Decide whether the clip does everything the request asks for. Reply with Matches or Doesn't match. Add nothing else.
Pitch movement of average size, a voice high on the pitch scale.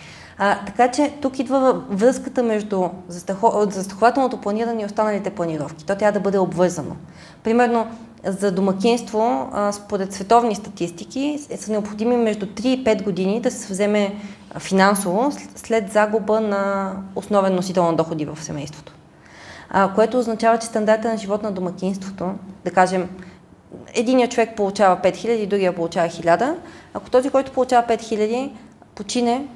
Matches